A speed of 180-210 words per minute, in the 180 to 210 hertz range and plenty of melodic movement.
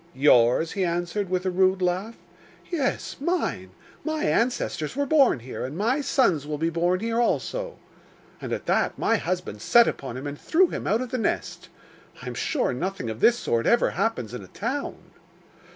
Yes: average, 185 wpm; high, 190 Hz; wide, 8.6 semitones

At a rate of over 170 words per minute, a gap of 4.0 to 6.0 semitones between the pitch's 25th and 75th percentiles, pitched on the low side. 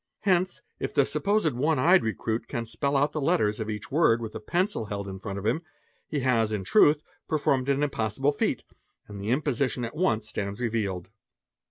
Yes: average, 200 wpm; wide, 5.6 semitones; low, 120 Hz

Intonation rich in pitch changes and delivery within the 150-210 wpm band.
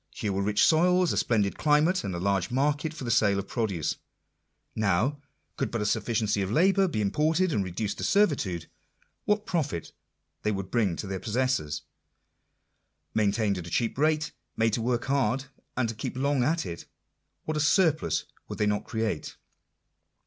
Yes: wide, 7.0 semitones; average, 180 wpm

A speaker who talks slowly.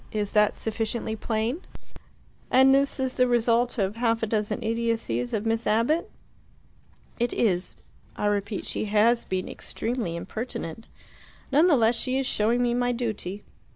No: average, 155 wpm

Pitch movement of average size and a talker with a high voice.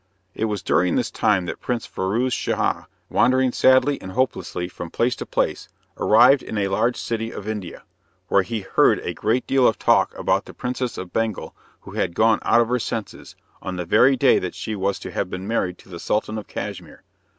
No: average, 4.6 semitones; low, 110 Hz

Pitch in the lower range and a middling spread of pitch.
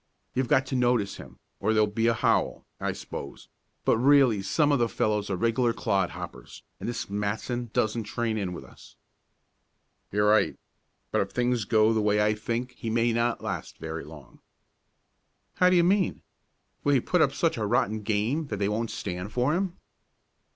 Yes: low, 115 Hz; average, 3.1 semitones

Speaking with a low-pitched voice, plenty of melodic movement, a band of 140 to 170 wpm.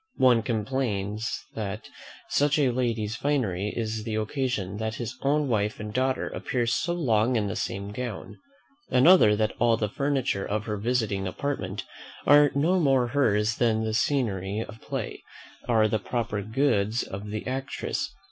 No: low, 110 Hz; average, 3.8 semitones; average, 160 wpm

